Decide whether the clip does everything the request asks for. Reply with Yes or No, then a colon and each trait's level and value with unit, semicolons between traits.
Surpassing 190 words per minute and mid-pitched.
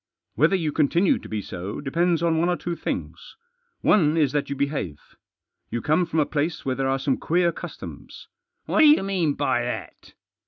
Yes: average, 200 wpm; medium, 155 Hz